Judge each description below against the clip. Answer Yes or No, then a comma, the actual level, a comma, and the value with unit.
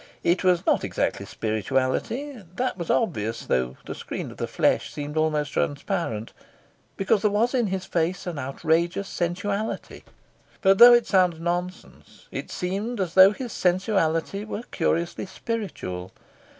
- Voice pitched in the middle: Yes, medium, 180 Hz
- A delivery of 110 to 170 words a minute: Yes, average, 145 wpm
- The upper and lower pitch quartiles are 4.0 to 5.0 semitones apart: Yes, average, 4.4 semitones